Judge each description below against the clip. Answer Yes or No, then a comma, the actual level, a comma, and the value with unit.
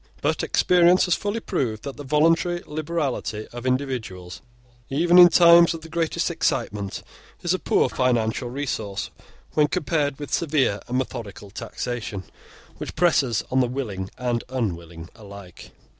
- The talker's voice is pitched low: Yes, low, 130 Hz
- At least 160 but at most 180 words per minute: No, average, 145 wpm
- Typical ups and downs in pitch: No, wide, 7.1 semitones